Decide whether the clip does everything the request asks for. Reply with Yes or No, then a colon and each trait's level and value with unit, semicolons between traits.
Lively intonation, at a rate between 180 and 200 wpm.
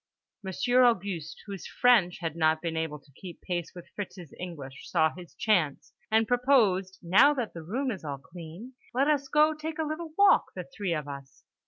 Yes: wide, 7.3 semitones; average, 190 wpm